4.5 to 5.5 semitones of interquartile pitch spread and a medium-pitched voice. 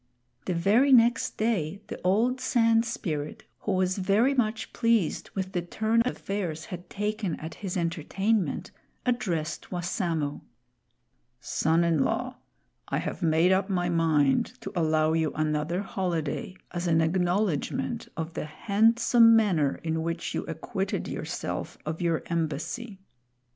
Yes: average, 5.0 semitones; medium, 180 Hz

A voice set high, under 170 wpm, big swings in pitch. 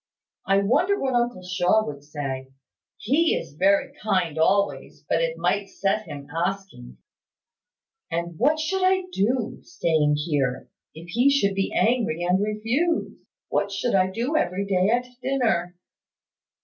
Yes: high, 200 Hz; average, 150 wpm; wide, 6.4 semitones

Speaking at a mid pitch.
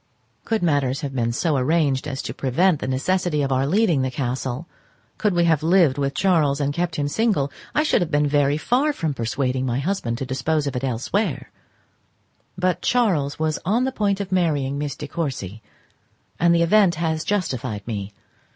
Yes: medium, 150 Hz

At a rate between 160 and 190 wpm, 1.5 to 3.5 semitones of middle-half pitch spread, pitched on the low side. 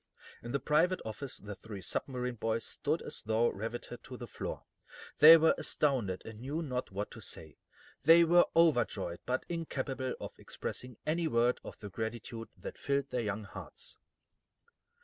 No: average, 165 wpm; average, 5.2 semitones; low, 125 Hz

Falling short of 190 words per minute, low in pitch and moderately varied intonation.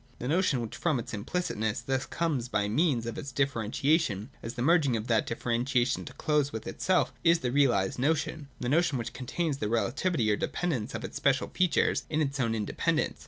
No: average, 200 wpm; low, 130 Hz; average, 4.8 semitones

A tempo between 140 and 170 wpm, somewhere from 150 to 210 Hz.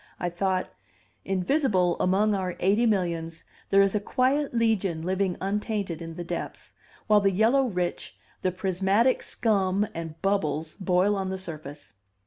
Yes: average, 145 wpm; high, 190 Hz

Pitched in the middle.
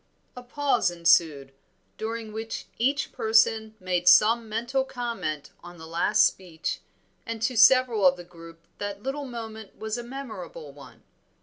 No: high, 220 Hz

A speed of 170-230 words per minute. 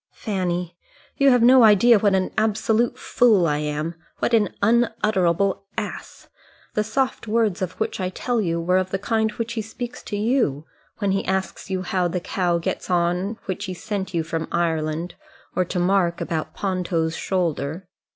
Yes: average, 175 wpm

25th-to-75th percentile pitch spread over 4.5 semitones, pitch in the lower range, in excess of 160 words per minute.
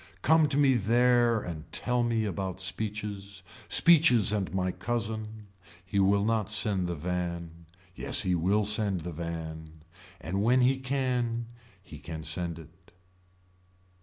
No: average, 5.1 semitones; low, 100 Hz; average, 140 wpm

